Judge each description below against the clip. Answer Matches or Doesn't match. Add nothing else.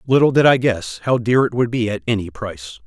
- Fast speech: Matches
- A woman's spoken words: Doesn't match